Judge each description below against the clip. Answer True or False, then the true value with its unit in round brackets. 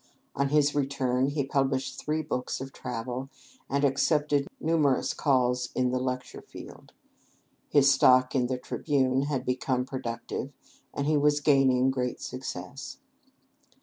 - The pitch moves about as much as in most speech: False (1.9 semitones)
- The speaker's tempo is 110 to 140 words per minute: True (135 wpm)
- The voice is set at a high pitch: False (135 Hz)